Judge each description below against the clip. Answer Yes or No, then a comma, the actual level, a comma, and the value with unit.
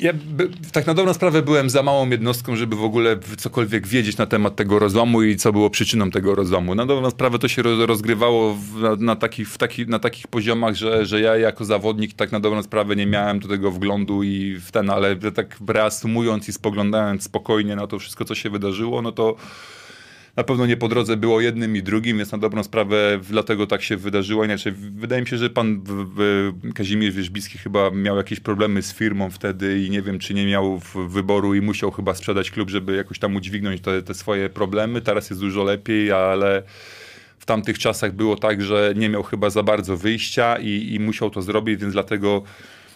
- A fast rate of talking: Yes, fast, 205 wpm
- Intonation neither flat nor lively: No, narrow, 2.1 semitones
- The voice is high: No, low, 105 Hz